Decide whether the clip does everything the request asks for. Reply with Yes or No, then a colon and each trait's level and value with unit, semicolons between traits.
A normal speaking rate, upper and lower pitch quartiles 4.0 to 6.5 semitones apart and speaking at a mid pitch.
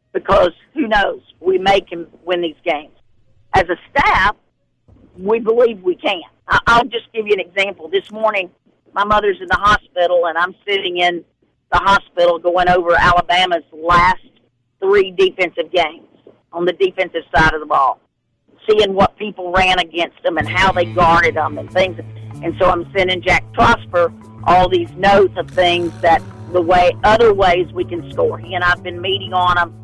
No: average, 175 wpm; average, 3.1 semitones; medium, 180 Hz